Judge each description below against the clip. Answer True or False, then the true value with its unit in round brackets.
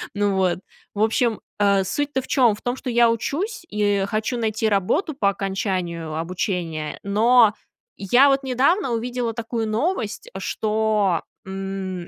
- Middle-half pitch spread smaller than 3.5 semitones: False (4.0 semitones)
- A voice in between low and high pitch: False (215 Hz)